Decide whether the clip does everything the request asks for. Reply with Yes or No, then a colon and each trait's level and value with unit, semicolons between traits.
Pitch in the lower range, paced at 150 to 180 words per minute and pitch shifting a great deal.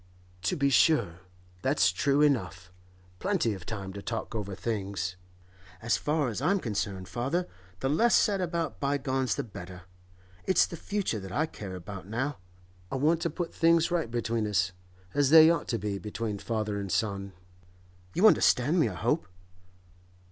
Yes: low, 115 Hz; average, 160 wpm; wide, 8.0 semitones